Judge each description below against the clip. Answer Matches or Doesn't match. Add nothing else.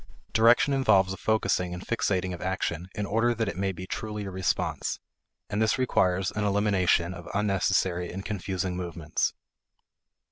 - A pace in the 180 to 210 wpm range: Doesn't match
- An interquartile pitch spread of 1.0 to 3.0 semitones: Matches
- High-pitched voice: Doesn't match